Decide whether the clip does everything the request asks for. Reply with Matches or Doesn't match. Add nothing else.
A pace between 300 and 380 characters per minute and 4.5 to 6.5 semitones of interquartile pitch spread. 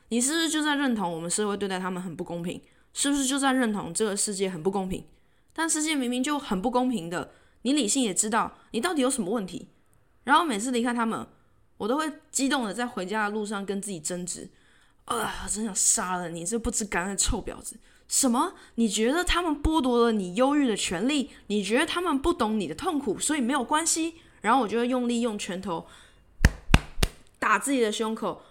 Matches